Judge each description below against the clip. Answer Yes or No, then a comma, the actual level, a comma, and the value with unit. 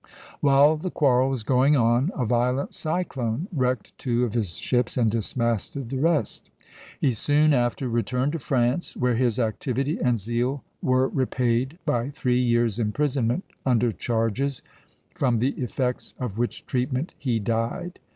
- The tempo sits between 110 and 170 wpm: Yes, average, 150 wpm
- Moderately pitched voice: No, low, 125 Hz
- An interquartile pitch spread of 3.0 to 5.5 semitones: No, narrow, 2.6 semitones